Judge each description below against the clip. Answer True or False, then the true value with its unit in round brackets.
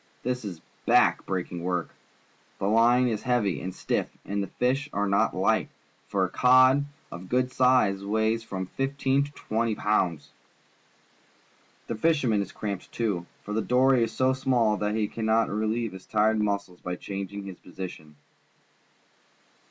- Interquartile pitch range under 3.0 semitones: False (4.3 semitones)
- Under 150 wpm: False (155 wpm)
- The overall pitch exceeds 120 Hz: False (110 Hz)